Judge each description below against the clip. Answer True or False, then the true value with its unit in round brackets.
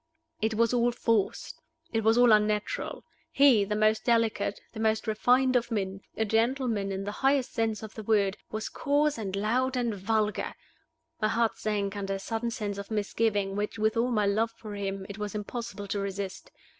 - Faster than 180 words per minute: True (190 wpm)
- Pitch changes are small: True (2.3 semitones)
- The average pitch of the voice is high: True (215 Hz)